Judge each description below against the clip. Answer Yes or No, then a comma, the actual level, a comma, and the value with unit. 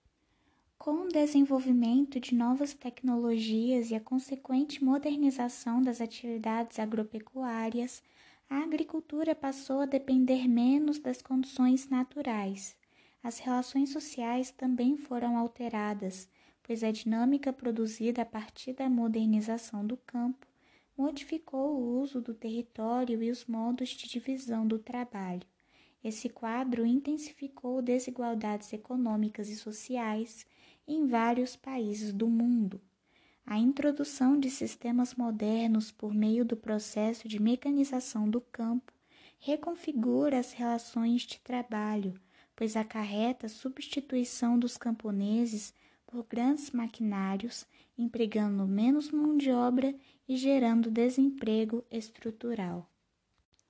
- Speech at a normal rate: No, slow, 110 wpm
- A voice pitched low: No, high, 240 Hz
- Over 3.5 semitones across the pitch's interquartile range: No, average, 2.8 semitones